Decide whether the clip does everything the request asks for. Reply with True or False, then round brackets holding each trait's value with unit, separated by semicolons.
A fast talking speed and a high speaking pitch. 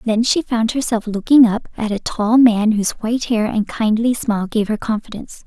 True (210 wpm; 225 Hz)